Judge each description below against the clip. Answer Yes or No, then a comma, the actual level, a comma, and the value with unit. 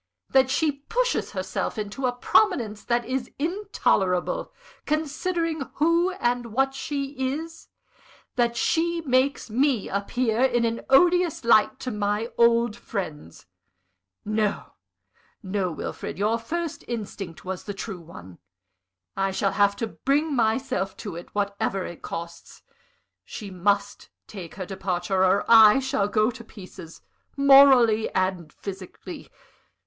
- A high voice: Yes, high, 230 Hz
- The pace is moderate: No, slow, 130 wpm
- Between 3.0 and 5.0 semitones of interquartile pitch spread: No, wide, 5.5 semitones